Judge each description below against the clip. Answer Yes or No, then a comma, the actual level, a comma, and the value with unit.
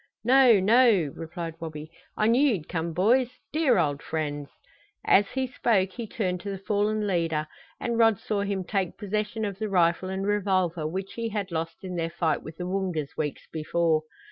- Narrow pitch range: No, average, 4.5 semitones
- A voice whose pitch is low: No, high, 190 Hz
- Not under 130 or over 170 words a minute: No, average, 185 wpm